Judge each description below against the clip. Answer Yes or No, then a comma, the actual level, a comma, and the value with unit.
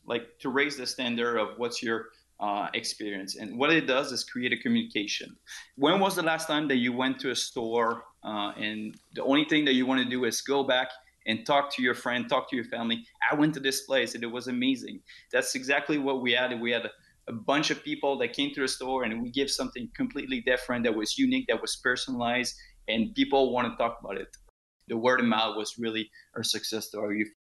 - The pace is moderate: No, fast, 230 wpm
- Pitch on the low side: Yes, low, 125 Hz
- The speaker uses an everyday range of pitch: Yes, average, 3.4 semitones